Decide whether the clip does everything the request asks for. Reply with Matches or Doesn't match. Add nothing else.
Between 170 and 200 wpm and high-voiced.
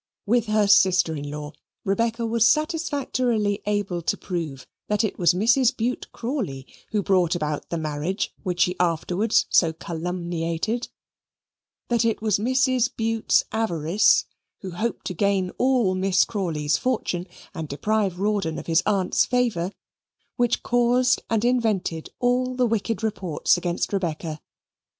Doesn't match